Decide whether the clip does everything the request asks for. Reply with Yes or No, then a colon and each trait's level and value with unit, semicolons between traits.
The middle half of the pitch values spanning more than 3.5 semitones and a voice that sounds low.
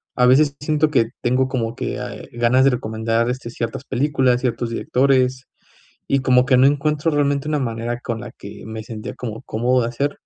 No: average, 2.8 semitones; low, 125 Hz